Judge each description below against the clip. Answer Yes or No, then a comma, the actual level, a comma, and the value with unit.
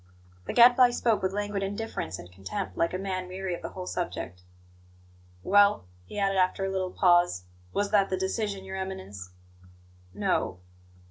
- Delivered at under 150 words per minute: No, average, 160 wpm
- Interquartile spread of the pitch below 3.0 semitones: Yes, narrow, 2.4 semitones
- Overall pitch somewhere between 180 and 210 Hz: Yes, high, 190 Hz